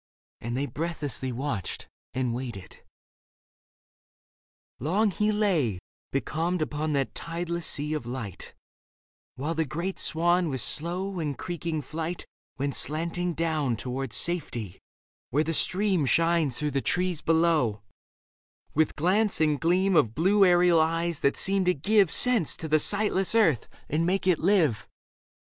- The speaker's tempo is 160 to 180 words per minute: No, average, 140 wpm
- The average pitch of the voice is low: No, medium, 160 Hz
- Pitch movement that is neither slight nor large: Yes, average, 4.1 semitones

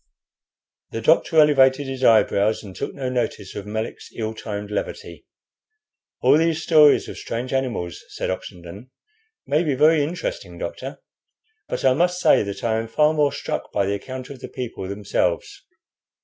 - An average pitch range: No, wide, 6.2 semitones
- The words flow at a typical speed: Yes, average, 165 wpm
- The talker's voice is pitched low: Yes, low, 130 Hz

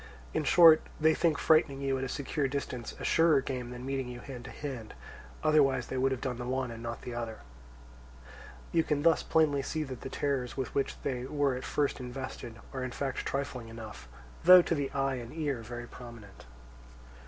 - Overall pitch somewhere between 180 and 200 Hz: No, low, 135 Hz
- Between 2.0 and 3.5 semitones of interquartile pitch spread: Yes, average, 2.8 semitones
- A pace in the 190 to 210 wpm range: Yes, average, 200 wpm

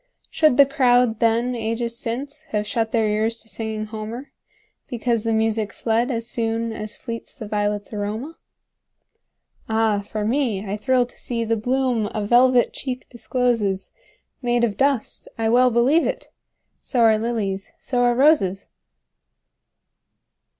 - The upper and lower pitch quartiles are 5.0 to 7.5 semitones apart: No, narrow, 2.4 semitones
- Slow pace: Yes, slow, 120 wpm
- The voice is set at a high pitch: Yes, high, 230 Hz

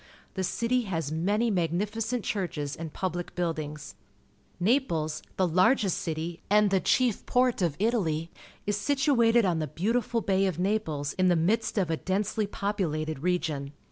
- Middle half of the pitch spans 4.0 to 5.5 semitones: Yes, average, 5.0 semitones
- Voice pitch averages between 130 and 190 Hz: Yes, medium, 185 Hz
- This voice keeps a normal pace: Yes, average, 150 wpm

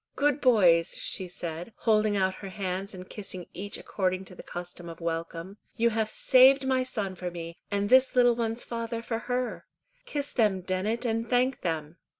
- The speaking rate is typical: Yes, average, 180 wpm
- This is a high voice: Yes, high, 205 Hz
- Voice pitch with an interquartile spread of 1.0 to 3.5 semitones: No, average, 4.6 semitones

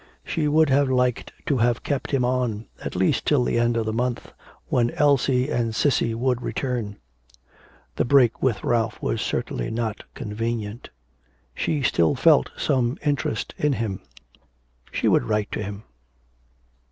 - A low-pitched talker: Yes, low, 120 Hz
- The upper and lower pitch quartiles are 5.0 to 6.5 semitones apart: No, average, 3.0 semitones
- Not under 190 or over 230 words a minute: No, average, 155 wpm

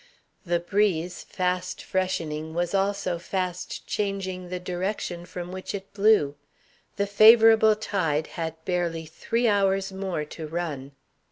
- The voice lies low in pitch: No, medium, 180 Hz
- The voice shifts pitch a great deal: No, average, 2.7 semitones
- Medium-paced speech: No, slow, 125 wpm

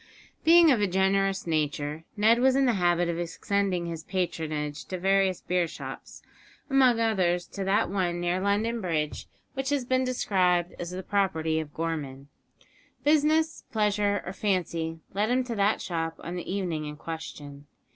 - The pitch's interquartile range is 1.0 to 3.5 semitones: No, average, 4.3 semitones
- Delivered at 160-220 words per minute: Yes, average, 165 wpm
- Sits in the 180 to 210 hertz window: Yes, medium, 185 Hz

